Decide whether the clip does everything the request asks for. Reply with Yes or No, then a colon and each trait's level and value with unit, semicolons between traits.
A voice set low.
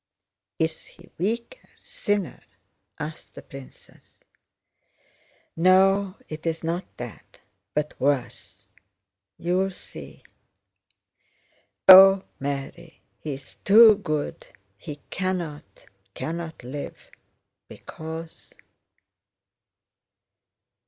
No: medium, 165 Hz